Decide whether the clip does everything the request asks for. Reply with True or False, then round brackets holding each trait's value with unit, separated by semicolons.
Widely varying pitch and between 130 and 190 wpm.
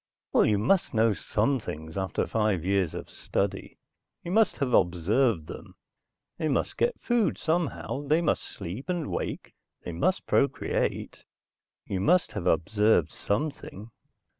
True (8.5 semitones; 140 wpm)